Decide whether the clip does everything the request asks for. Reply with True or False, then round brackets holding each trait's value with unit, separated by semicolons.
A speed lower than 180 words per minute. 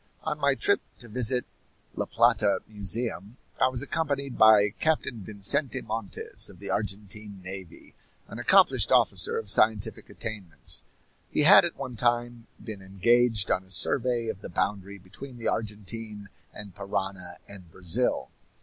True (145 wpm)